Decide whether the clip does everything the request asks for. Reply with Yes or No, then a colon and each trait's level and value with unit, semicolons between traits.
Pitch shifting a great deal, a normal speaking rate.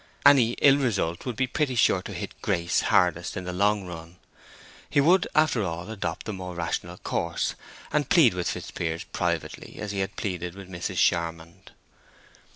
Yes: wide, 5.9 semitones; average, 170 wpm